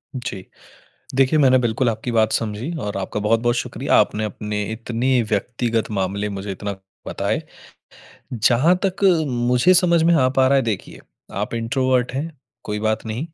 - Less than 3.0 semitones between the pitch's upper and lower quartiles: No, average, 3.6 semitones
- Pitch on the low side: Yes, low, 120 Hz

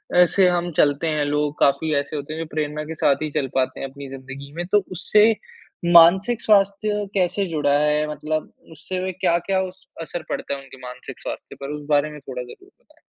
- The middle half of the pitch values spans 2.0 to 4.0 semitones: No, average, 4.4 semitones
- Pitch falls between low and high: Yes, medium, 155 Hz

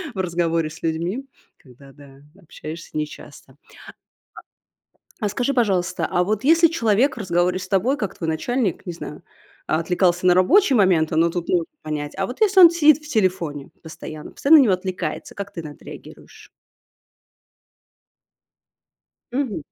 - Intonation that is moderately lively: No, wide, 6.8 semitones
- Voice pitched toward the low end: No, medium, 185 Hz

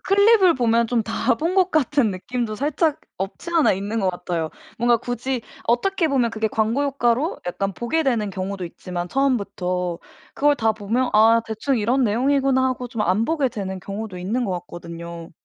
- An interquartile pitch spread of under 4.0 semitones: No, wide, 5.4 semitones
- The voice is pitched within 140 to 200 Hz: No, high, 230 Hz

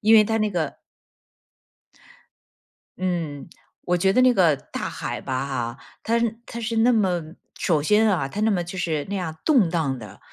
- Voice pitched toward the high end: No, medium, 180 Hz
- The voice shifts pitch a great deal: Yes, wide, 5.8 semitones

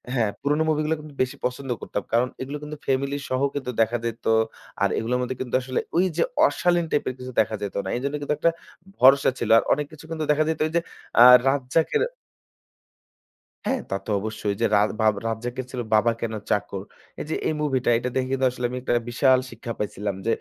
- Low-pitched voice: Yes, low, 130 Hz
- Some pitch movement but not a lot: Yes, average, 3.8 semitones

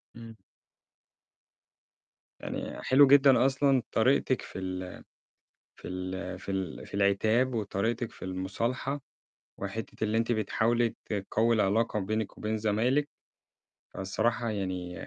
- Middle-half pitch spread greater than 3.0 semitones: Yes, average, 3.7 semitones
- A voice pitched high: No, low, 110 Hz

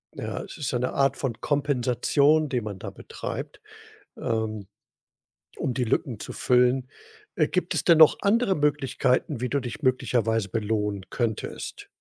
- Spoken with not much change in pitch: No, average, 4.2 semitones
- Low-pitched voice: Yes, low, 125 Hz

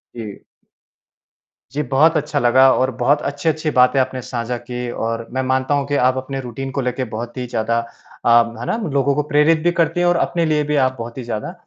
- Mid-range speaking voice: No, low, 130 Hz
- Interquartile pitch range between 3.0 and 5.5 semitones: Yes, average, 3.5 semitones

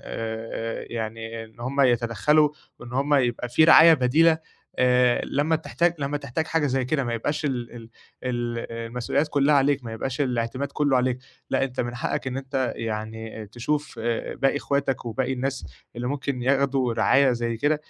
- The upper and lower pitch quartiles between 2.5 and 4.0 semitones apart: Yes, average, 3.1 semitones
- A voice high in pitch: No, low, 130 Hz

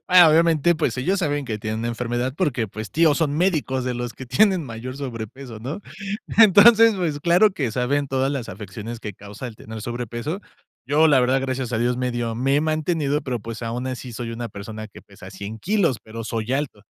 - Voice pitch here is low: Yes, low, 130 Hz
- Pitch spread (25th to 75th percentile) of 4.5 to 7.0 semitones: Yes, average, 4.9 semitones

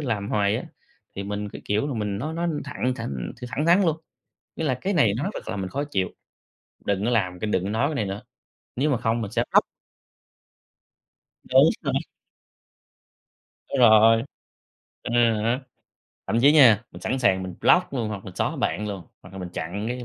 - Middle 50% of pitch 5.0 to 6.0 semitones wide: Yes, average, 5.3 semitones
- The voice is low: Yes, low, 115 Hz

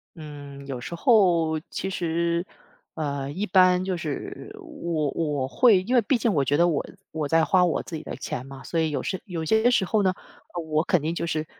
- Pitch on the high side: No, medium, 170 Hz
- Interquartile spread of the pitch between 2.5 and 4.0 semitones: Yes, average, 3.7 semitones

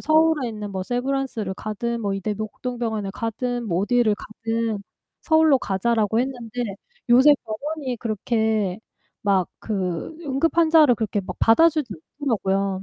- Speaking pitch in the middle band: No, high, 225 Hz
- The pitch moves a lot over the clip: No, average, 4.1 semitones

